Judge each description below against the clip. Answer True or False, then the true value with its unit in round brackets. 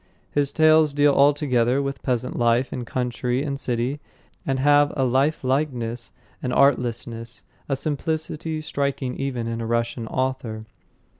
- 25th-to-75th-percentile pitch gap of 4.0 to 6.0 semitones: False (3.2 semitones)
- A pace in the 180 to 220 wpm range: False (135 wpm)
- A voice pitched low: True (130 Hz)